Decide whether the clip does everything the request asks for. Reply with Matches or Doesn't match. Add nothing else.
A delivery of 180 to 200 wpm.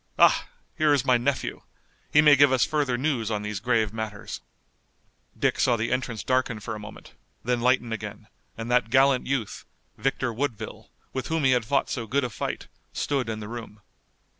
Matches